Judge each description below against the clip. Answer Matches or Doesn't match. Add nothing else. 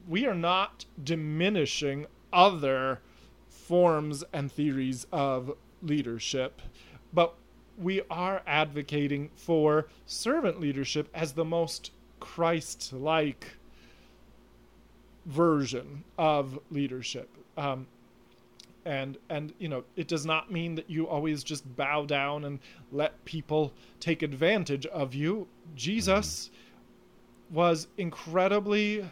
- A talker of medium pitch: Matches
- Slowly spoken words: Matches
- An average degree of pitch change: Matches